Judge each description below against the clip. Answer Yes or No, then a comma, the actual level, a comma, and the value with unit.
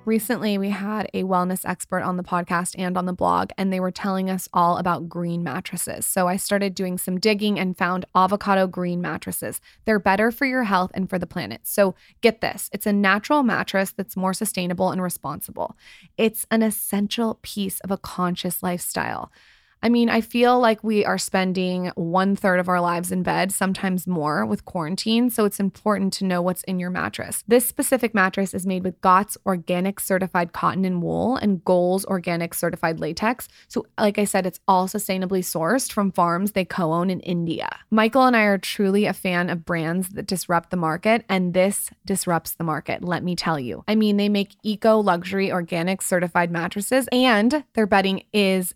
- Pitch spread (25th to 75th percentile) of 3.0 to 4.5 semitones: No, narrow, 2.5 semitones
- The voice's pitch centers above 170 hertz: Yes, high, 190 Hz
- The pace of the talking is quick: No, average, 195 wpm